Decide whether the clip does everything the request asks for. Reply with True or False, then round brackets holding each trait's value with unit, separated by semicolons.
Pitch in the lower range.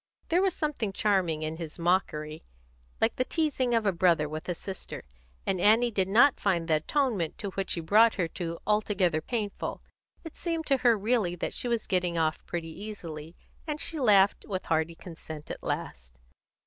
False (190 Hz)